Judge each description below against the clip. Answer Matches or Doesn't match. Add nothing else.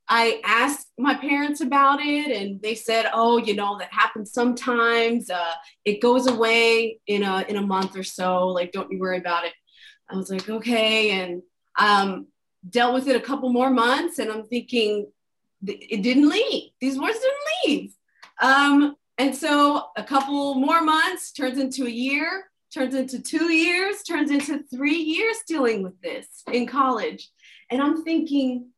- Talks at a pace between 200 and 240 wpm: Doesn't match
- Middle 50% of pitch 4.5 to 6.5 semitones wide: Matches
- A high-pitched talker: Matches